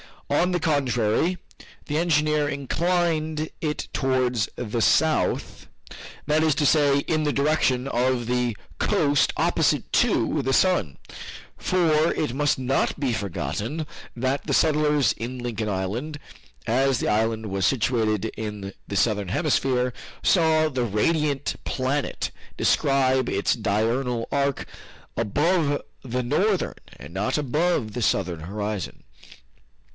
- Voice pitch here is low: Yes, low, 130 Hz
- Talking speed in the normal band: No, slow, 125 wpm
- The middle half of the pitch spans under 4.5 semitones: No, average, 5.1 semitones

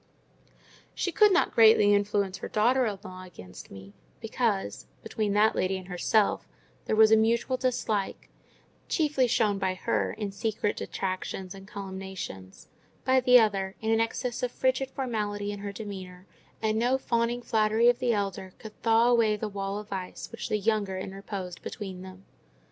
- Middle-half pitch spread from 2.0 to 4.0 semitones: Yes, average, 3.2 semitones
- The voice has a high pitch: Yes, high, 210 Hz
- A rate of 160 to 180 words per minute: Yes, average, 165 wpm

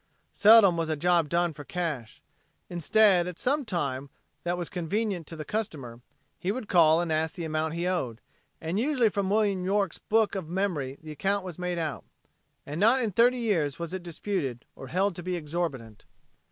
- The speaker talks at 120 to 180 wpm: No, average, 190 wpm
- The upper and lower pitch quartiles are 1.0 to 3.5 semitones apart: No, average, 4.3 semitones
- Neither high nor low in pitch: Yes, medium, 175 Hz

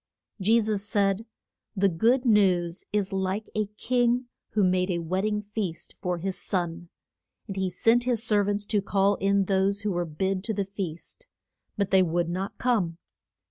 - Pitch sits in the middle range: No, high, 195 Hz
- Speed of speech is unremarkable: Yes, average, 180 wpm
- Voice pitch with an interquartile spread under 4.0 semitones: Yes, narrow, 2.6 semitones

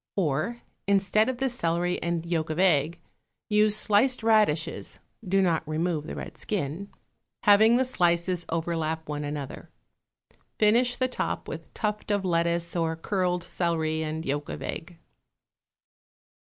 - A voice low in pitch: No, medium, 175 Hz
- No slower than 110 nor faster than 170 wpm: Yes, average, 140 wpm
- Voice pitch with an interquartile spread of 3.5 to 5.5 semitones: Yes, average, 4.5 semitones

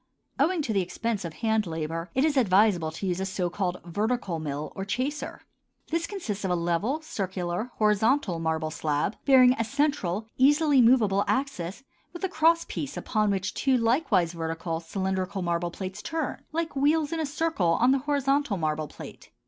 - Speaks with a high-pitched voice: Yes, high, 210 Hz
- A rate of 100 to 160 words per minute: No, average, 175 wpm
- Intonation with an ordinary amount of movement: No, wide, 7.9 semitones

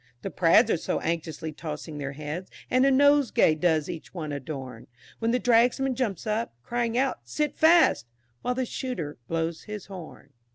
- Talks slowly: No, average, 170 wpm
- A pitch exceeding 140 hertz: Yes, medium, 185 Hz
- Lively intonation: Yes, wide, 8.2 semitones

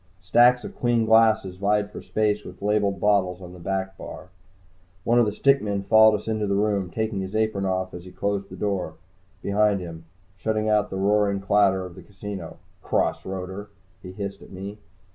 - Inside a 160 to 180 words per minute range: No, average, 195 wpm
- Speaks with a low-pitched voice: Yes, low, 100 Hz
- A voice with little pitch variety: Yes, narrow, 2.0 semitones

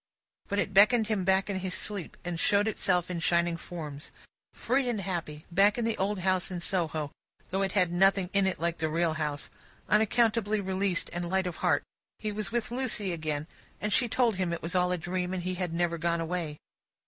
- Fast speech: Yes, fast, 210 wpm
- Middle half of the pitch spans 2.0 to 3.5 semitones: Yes, average, 3.0 semitones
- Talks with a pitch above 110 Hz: Yes, medium, 185 Hz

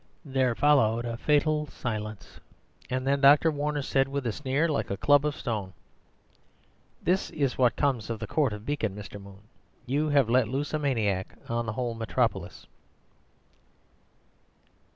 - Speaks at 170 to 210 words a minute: No, average, 155 wpm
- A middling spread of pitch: Yes, average, 4.4 semitones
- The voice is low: Yes, low, 130 Hz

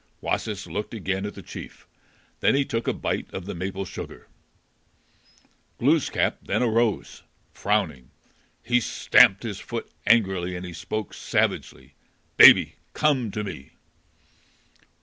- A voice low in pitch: Yes, low, 105 Hz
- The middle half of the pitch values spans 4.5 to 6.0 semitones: No, average, 3.8 semitones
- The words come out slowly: Yes, slow, 130 wpm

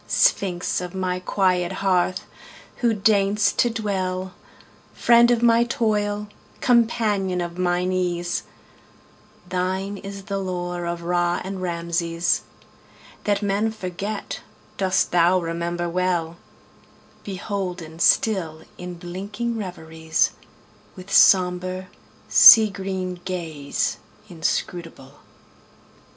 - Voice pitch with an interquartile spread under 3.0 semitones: Yes, narrow, 2.4 semitones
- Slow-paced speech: Yes, slow, 85 wpm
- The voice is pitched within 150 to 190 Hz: Yes, medium, 185 Hz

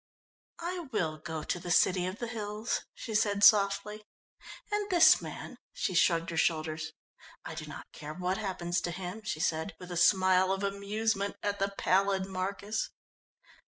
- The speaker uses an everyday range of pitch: Yes, average, 3.1 semitones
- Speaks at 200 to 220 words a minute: No, average, 165 wpm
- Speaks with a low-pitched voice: No, high, 195 Hz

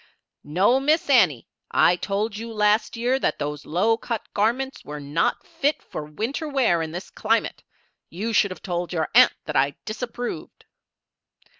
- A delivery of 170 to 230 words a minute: No, average, 160 wpm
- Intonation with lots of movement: Yes, wide, 6.3 semitones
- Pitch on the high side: Yes, high, 210 Hz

